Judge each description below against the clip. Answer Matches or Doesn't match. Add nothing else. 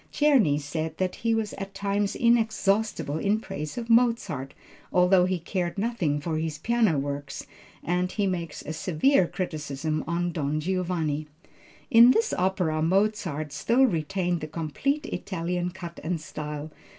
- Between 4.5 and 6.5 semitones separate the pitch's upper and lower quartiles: Matches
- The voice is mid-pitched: Matches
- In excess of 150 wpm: Doesn't match